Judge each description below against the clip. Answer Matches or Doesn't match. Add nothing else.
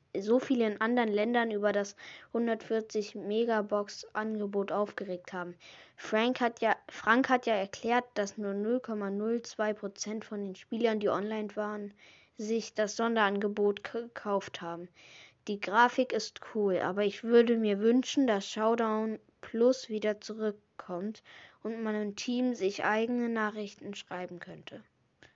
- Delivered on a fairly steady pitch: Matches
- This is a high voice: Matches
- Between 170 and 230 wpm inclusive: Doesn't match